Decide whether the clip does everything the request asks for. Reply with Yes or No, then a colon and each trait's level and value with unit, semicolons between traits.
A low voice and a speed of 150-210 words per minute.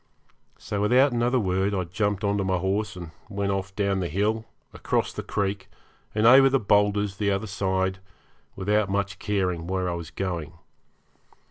Yes: low, 100 Hz; average, 170 wpm